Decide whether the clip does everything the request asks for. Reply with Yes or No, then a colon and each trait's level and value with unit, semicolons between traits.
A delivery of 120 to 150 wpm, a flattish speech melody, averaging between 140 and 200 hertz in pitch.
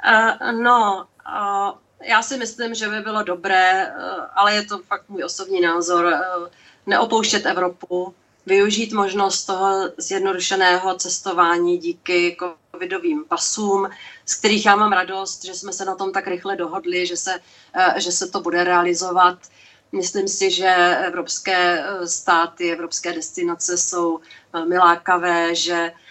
Yes: average, 125 wpm; narrow, 2.2 semitones; medium, 185 Hz